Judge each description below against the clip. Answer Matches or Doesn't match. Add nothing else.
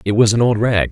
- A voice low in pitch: Matches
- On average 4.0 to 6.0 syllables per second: Doesn't match